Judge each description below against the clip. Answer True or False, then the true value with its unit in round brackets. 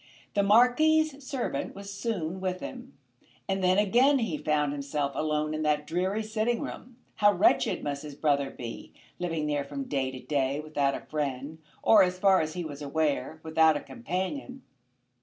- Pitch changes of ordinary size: False (5.9 semitones)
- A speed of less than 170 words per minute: False (175 wpm)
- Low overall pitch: False (160 Hz)